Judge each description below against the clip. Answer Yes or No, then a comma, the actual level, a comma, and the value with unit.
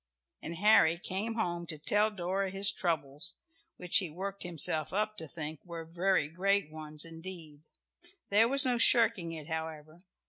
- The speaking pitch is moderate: Yes, medium, 175 Hz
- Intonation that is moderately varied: Yes, average, 3.8 semitones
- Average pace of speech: Yes, average, 160 wpm